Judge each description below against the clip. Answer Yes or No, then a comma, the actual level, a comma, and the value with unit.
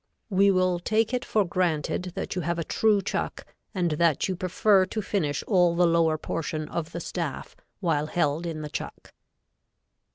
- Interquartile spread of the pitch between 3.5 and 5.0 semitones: No, average, 2.7 semitones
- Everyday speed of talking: Yes, average, 175 wpm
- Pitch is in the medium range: Yes, medium, 175 Hz